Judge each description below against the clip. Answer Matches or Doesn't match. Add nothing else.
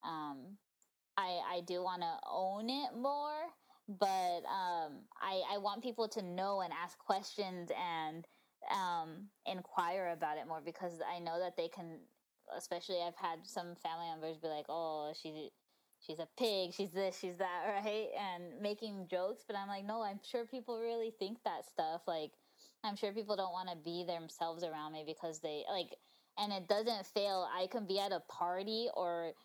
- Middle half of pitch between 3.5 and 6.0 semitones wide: Matches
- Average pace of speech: Matches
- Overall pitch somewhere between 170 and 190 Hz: Matches